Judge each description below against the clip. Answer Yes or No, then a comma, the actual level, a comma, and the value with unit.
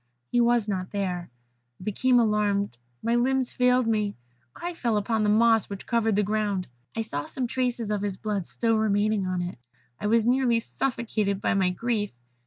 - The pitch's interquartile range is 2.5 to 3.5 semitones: Yes, average, 2.8 semitones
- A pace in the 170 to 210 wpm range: Yes, average, 185 wpm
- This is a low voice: No, high, 215 Hz